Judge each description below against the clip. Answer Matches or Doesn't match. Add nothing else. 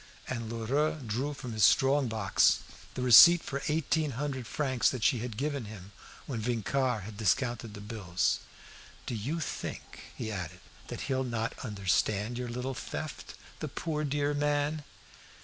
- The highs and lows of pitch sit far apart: Doesn't match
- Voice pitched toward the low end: Matches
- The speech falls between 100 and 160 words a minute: Matches